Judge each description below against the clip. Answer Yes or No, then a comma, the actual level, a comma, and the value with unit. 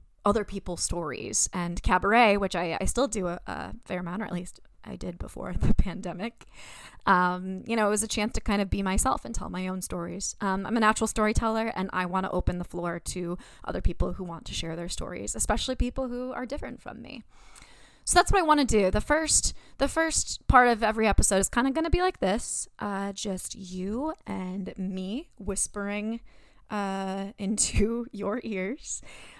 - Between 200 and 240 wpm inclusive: Yes, fast, 205 wpm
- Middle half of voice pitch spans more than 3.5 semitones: Yes, average, 4.1 semitones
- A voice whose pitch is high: Yes, high, 205 Hz